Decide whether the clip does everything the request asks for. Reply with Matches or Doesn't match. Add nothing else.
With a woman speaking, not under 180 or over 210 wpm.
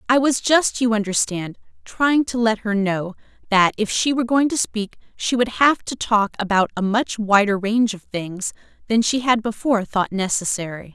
Matches